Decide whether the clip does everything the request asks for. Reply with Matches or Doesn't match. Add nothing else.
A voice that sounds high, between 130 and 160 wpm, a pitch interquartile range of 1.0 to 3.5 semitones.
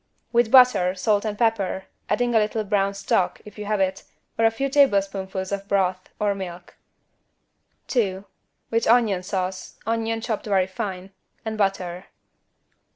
Matches